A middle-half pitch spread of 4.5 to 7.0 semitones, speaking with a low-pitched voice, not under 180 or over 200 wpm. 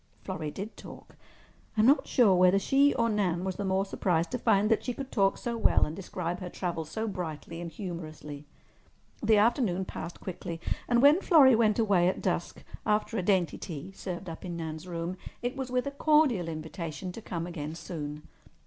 No: average, 5.1 semitones; high, 190 Hz; average, 195 wpm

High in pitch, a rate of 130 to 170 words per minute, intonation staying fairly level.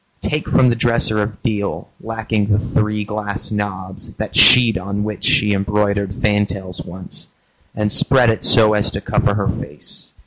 No: low, 105 Hz; average, 165 wpm; narrow, 1.7 semitones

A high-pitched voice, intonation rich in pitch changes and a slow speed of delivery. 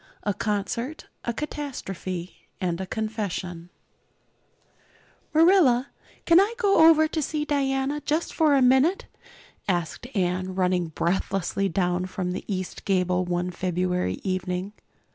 Yes: high, 195 Hz; wide, 7.8 semitones; slow, 125 wpm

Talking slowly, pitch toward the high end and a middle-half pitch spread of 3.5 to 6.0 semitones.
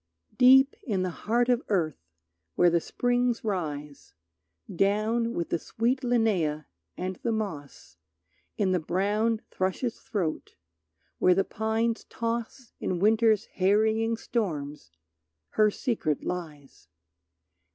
Yes: slow, 115 wpm; high, 210 Hz; average, 5.1 semitones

